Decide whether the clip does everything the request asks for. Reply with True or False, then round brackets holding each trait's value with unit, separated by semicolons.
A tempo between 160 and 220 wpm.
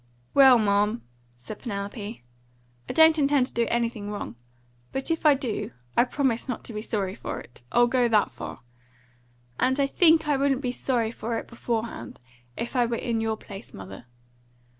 True (180 wpm)